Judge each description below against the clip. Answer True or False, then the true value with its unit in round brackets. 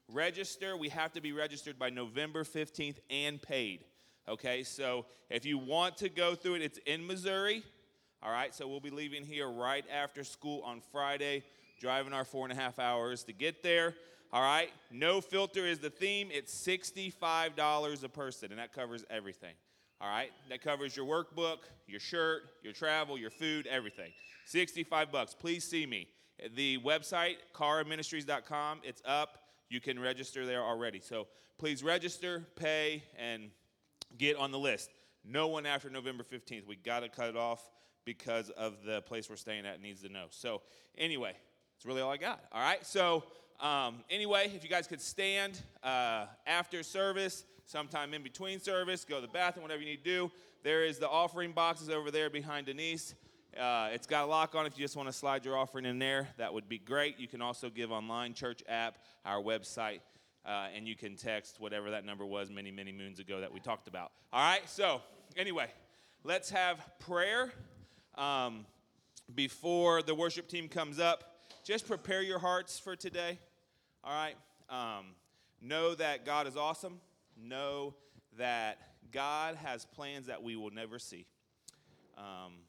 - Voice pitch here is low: False (145 Hz)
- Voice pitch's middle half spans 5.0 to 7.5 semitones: True (5.5 semitones)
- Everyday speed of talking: True (180 wpm)